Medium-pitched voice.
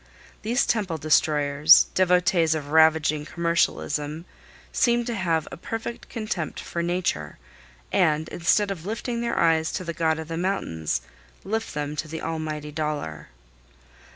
Yes: medium, 160 Hz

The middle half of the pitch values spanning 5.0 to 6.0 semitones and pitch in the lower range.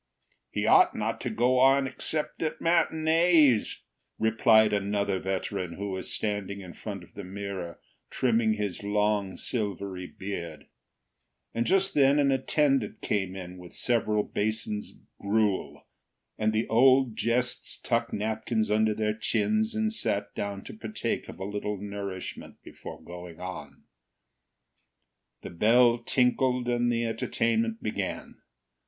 No: average, 3.9 semitones; low, 110 Hz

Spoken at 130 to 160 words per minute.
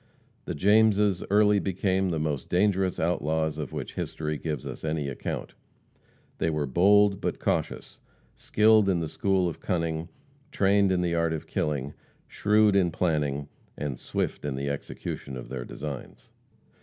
Yes: average, 155 wpm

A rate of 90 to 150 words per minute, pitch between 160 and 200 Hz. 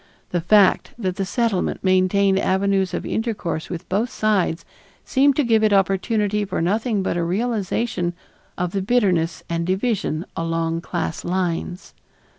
Yes: average, 145 wpm; high, 190 Hz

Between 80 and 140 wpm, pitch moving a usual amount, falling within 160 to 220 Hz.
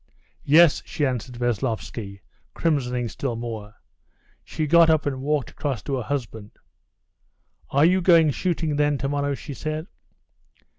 No: slow, 135 wpm; average, 4.1 semitones; medium, 140 Hz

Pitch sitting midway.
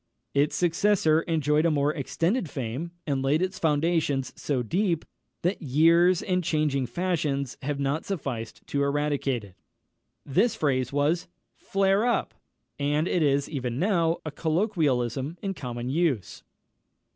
Yes: medium, 150 Hz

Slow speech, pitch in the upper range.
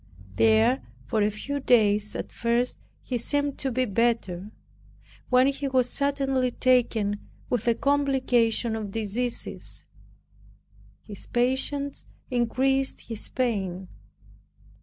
Yes: slow, 110 wpm; high, 240 Hz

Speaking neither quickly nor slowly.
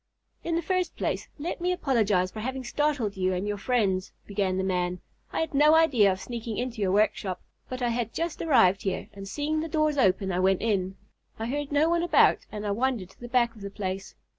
No: fast, 225 wpm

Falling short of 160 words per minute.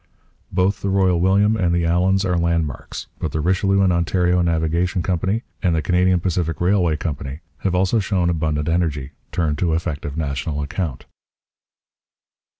Yes: average, 150 wpm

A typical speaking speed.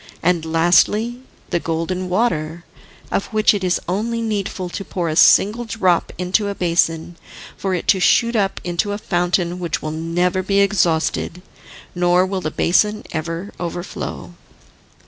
Yes: average, 150 wpm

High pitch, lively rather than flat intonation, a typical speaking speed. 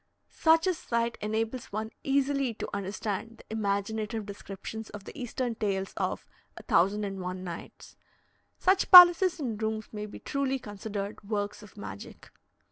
No: high, 220 Hz; average, 3.7 semitones; average, 150 wpm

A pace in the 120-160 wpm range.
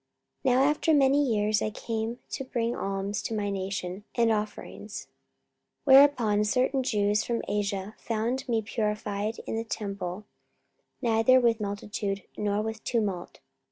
Yes: average, 145 wpm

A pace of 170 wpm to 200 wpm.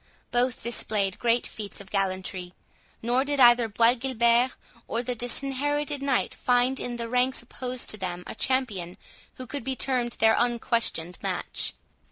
No: average, 155 wpm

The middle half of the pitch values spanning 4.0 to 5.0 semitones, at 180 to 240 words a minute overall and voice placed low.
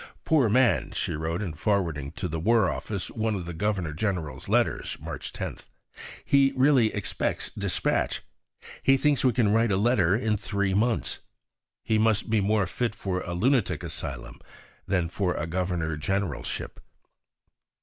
No: average, 4.5 semitones; average, 155 wpm; low, 100 Hz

